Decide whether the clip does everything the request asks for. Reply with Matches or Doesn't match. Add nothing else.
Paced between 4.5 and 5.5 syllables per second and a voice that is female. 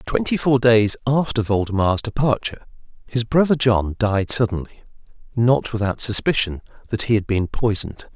Doesn't match